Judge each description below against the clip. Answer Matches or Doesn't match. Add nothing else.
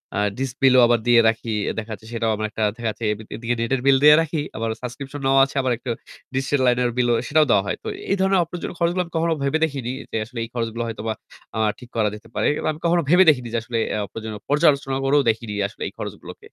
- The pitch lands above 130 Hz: Doesn't match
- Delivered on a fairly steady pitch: Doesn't match